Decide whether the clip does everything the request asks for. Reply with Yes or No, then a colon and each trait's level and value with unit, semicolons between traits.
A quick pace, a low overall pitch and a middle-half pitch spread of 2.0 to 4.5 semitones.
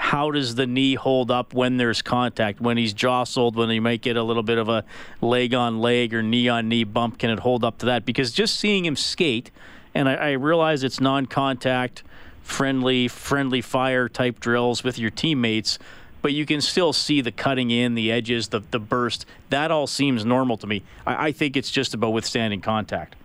Yes: fast, 210 wpm; low, 125 Hz; narrow, 2.4 semitones